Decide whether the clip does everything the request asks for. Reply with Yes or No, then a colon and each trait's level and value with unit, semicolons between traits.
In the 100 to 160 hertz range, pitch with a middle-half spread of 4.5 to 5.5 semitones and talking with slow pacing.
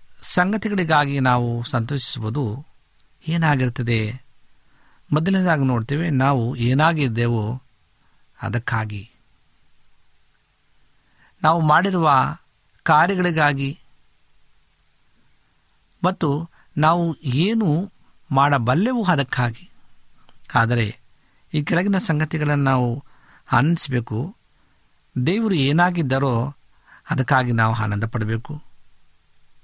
Yes: medium, 140 Hz; average, 5.1 semitones; slow, 60 wpm